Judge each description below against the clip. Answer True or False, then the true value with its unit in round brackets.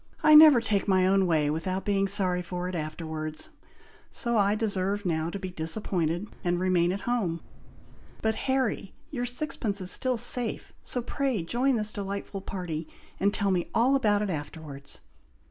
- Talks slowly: False (165 wpm)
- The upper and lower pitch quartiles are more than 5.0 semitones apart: False (4.3 semitones)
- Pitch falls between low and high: False (195 Hz)